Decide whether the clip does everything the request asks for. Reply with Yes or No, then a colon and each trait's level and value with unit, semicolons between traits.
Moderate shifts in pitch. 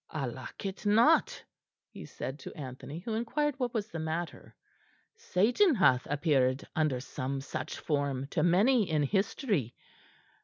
No: wide, 8.2 semitones